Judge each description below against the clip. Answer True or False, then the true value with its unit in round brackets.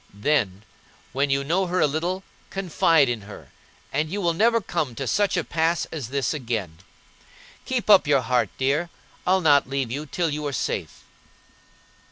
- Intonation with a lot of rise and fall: False (4.7 semitones)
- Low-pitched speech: False (150 Hz)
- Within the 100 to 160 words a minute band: False (175 wpm)